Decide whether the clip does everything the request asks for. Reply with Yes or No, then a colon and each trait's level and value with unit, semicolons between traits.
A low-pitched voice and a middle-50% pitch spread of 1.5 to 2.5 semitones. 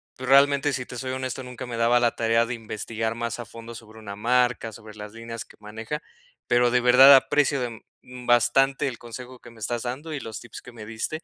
Yes: low, 120 Hz; narrow, 2.2 semitones